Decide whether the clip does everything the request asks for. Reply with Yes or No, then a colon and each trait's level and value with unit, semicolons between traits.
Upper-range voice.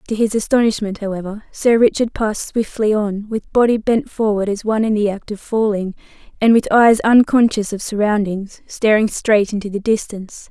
Yes: high, 215 Hz